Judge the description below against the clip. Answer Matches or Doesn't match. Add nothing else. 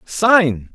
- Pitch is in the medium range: Matches